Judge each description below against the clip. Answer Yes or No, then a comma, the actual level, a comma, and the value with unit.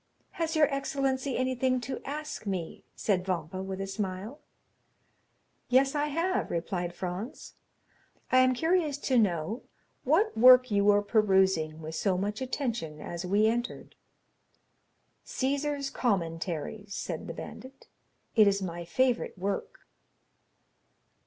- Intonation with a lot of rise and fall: Yes, wide, 6.2 semitones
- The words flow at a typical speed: No, slow, 125 wpm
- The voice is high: Yes, high, 220 Hz